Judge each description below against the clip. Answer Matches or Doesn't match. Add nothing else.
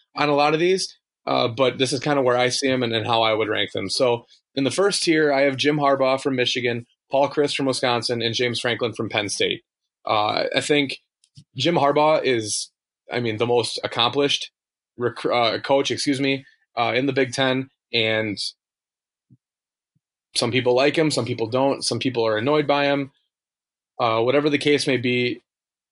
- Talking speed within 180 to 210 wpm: Matches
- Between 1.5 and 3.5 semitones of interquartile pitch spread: Matches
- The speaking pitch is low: Matches